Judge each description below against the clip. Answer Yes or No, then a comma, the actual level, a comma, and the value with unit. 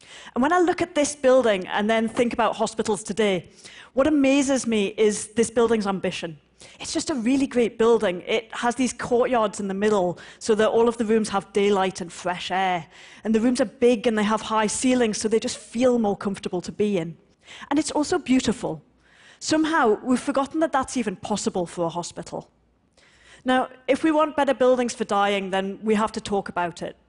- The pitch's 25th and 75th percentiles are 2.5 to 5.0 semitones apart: Yes, average, 4.4 semitones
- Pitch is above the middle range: Yes, high, 225 Hz